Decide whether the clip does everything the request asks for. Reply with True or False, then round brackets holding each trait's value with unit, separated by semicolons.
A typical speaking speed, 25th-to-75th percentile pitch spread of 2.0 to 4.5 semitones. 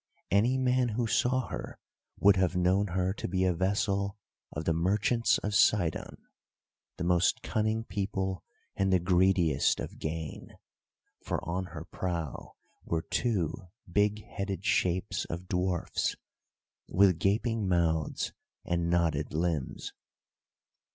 False (120 wpm; 3.0 semitones)